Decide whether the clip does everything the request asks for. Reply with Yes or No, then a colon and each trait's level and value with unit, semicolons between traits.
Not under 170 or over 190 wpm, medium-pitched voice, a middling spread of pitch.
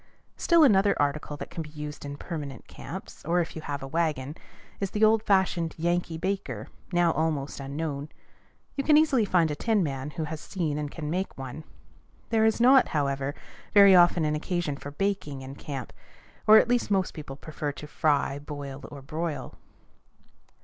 Yes: average, 175 wpm; medium, 155 Hz; average, 4.8 semitones